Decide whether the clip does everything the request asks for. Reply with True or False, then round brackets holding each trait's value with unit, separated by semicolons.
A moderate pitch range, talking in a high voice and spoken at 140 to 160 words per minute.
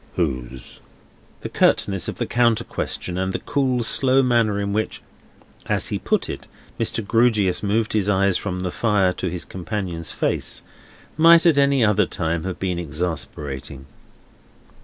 False (4.7 semitones; 100 Hz; 155 wpm)